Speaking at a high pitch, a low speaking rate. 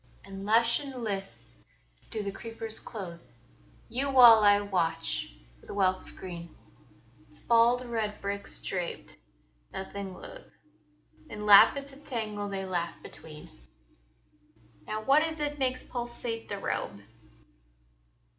Yes: high, 210 Hz; slow, 125 wpm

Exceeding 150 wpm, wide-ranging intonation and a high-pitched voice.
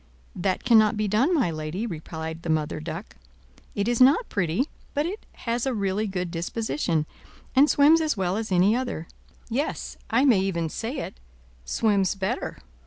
Yes: average, 170 wpm; wide, 6.5 semitones; high, 205 Hz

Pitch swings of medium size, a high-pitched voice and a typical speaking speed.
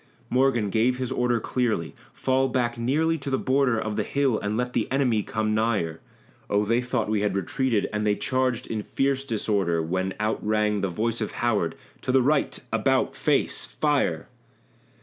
No: average, 3.6 semitones; low, 115 Hz; average, 180 wpm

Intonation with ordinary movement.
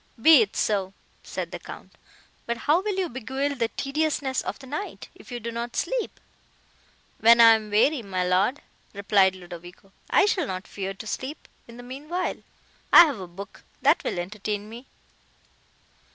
No: wide, 6.1 semitones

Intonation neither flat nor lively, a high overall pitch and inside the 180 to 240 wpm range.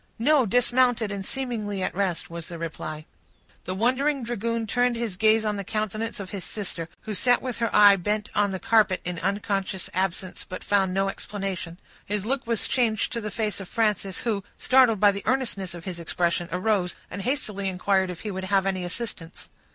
Yes: average, 3.4 semitones; high, 205 Hz; average, 195 wpm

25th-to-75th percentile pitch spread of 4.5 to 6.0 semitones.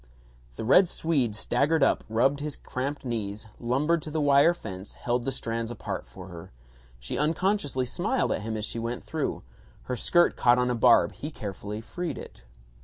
Yes: average, 5.1 semitones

